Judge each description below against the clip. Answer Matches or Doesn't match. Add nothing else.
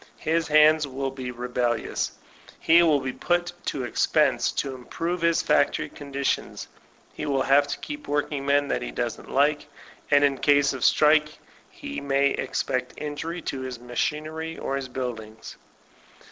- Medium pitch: Matches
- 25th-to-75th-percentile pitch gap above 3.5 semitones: Doesn't match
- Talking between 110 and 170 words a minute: Matches